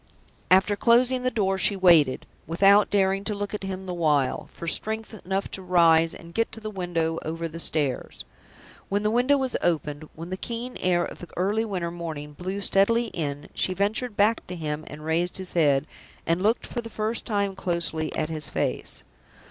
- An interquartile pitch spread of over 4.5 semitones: No, average, 4.1 semitones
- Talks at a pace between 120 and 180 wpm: No, average, 195 wpm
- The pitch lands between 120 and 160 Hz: No, medium, 185 Hz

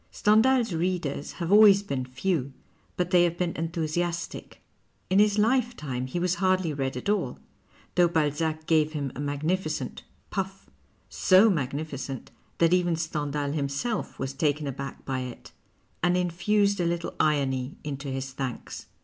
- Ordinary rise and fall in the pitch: Yes, average, 4.7 semitones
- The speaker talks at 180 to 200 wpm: No, average, 160 wpm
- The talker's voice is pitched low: No, medium, 160 Hz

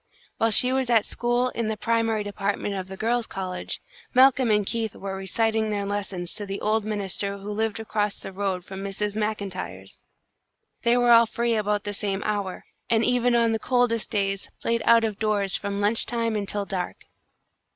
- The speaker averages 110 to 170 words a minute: No, average, 185 wpm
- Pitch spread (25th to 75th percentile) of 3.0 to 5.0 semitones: No, narrow, 2.5 semitones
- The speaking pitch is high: Yes, high, 210 Hz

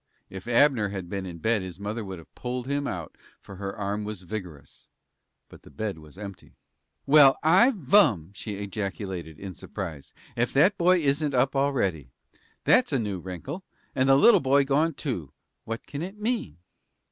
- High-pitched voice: No, low, 110 Hz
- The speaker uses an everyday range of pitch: No, wide, 6.9 semitones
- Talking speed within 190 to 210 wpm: No, average, 175 wpm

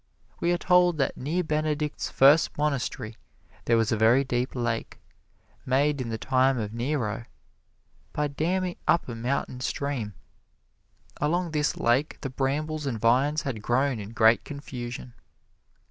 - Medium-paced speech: Yes, average, 145 wpm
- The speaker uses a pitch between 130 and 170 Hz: Yes, low, 135 Hz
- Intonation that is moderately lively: Yes, average, 4.2 semitones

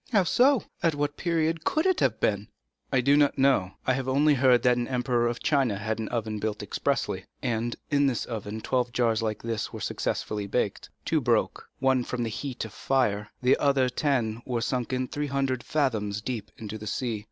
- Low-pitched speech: Yes, low, 125 Hz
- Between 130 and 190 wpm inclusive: No, average, 200 wpm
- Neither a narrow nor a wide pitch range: Yes, average, 3.9 semitones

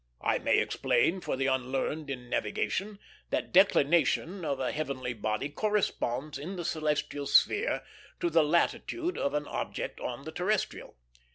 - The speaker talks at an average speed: Yes, average, 150 wpm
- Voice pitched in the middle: Yes, medium, 150 Hz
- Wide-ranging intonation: Yes, wide, 5.7 semitones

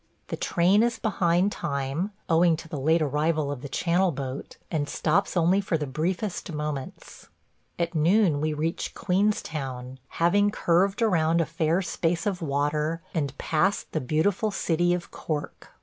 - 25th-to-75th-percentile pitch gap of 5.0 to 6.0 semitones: No, average, 3.3 semitones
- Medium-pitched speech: Yes, medium, 165 Hz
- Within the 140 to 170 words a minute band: Yes, average, 155 wpm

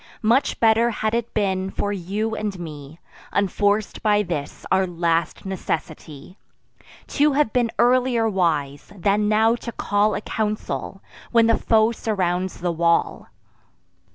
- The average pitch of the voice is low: No, high, 205 Hz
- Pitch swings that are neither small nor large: Yes, average, 4.1 semitones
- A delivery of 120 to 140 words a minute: Yes, slow, 135 wpm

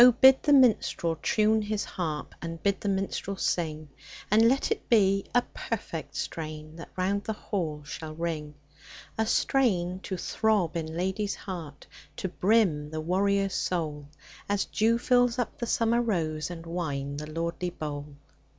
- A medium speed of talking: Yes, average, 155 wpm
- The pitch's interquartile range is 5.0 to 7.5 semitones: Yes, average, 5.3 semitones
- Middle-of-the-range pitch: Yes, medium, 180 Hz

